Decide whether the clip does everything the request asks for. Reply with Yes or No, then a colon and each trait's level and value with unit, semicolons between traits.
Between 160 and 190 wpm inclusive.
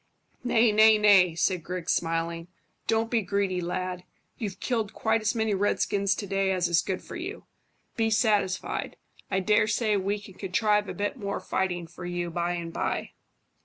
Yes: average, 175 wpm